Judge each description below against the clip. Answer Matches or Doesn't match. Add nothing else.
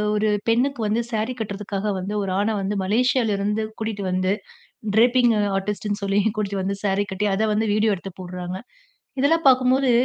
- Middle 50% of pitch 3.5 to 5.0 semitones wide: Doesn't match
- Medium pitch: Doesn't match